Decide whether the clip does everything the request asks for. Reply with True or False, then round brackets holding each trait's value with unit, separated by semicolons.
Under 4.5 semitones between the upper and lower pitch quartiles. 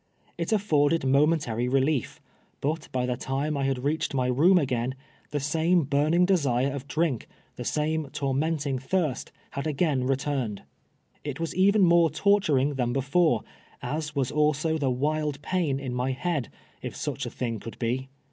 True (3.4 semitones)